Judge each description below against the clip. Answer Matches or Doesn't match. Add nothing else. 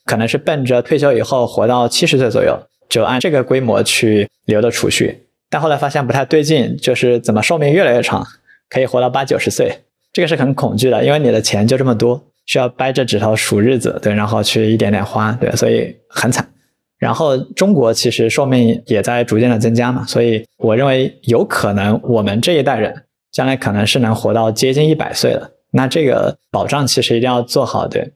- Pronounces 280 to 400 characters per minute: Matches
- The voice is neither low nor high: Doesn't match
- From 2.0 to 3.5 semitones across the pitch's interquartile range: Matches